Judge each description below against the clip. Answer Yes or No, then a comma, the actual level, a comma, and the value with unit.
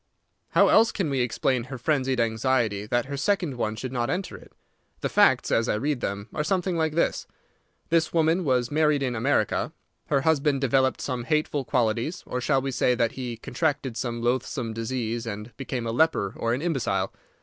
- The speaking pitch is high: No, low, 130 Hz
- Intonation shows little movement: No, average, 4.3 semitones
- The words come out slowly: No, average, 190 wpm